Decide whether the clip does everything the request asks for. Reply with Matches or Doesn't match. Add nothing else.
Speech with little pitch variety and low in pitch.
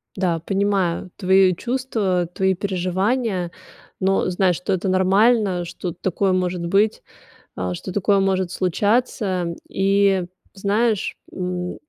Doesn't match